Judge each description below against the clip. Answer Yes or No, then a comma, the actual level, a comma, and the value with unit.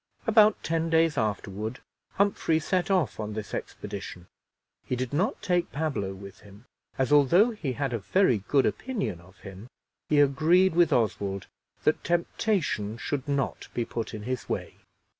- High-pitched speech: No, medium, 140 Hz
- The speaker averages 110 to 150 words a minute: No, average, 160 wpm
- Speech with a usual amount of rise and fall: No, wide, 8.0 semitones